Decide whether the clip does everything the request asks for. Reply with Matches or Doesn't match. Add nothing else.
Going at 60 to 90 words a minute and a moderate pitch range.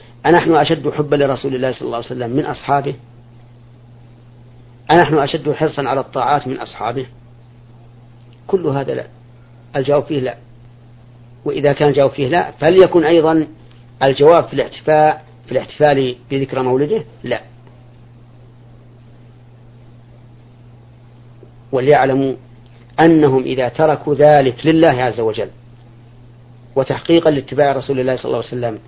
Doesn't match